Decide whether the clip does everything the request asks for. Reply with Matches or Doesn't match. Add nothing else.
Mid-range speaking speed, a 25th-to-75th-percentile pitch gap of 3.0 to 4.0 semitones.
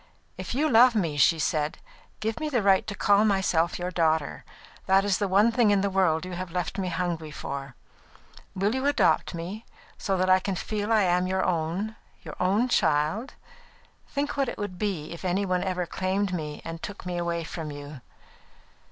Matches